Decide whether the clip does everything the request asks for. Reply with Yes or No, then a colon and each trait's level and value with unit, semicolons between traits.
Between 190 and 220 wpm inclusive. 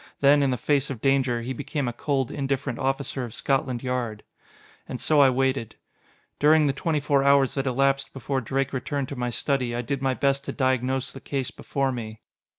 Yes: average, 200 wpm